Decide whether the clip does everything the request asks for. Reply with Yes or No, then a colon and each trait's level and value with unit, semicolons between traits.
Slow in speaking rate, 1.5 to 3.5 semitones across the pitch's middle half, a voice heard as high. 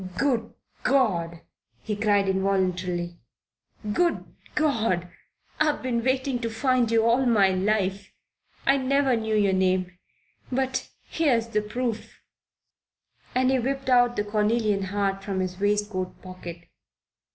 No: slow, 125 wpm; average, 4.8 semitones; high, 215 Hz